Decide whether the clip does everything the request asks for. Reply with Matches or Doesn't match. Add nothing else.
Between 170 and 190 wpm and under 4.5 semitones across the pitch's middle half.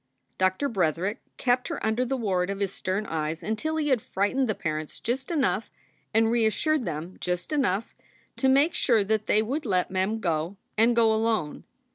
Doesn't match